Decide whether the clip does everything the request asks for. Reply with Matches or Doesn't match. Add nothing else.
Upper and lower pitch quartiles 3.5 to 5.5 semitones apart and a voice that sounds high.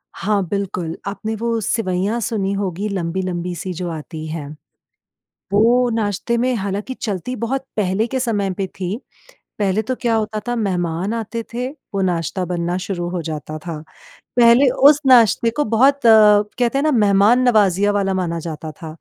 Matches